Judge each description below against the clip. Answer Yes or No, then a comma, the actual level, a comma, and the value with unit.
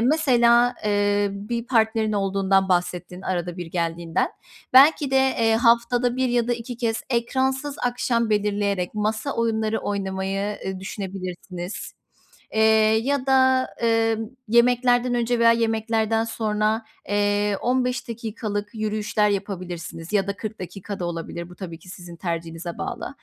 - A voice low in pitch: No, high, 215 Hz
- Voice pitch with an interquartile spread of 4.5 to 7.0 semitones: No, average, 3.7 semitones